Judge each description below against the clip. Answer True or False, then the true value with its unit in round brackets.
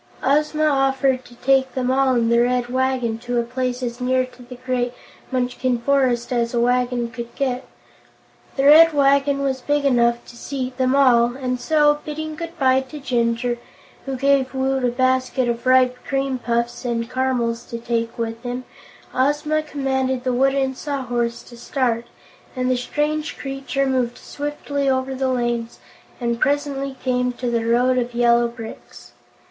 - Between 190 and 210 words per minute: False (165 wpm)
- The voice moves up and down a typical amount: False (2.1 semitones)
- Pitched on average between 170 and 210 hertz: False (255 Hz)